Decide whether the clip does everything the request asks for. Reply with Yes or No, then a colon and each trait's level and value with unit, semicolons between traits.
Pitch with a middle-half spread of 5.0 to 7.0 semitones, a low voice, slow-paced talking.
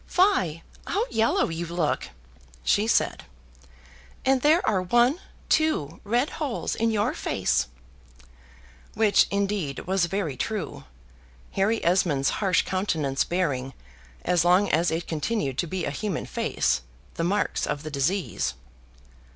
No: wide, 5.4 semitones; medium, 185 Hz; slow, 130 wpm